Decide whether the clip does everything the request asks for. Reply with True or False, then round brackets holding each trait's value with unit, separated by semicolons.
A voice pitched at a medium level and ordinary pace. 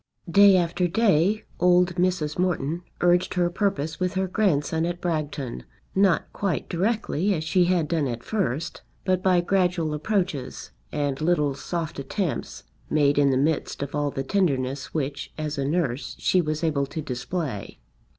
True (165 Hz; 160 wpm)